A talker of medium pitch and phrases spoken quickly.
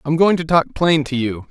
Yes: medium, 150 Hz; fast, 280 wpm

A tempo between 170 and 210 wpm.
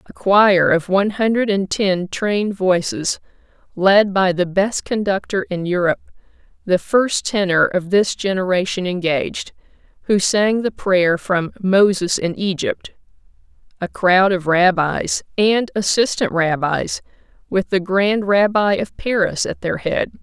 No: slow, 135 wpm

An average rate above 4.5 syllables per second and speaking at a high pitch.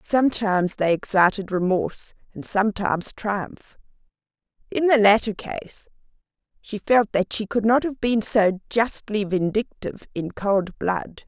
No: 4.4 syllables/s; high, 205 Hz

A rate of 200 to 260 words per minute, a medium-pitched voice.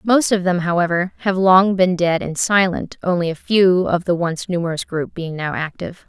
Yes: fast, 205 wpm; medium, 180 Hz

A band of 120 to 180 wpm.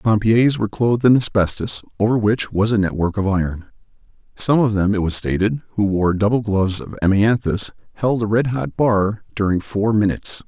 No: average, 190 wpm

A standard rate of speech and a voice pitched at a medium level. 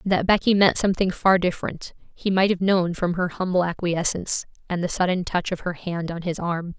No: fast, 210 wpm; medium, 180 Hz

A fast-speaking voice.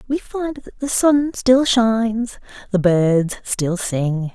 No: average, 150 wpm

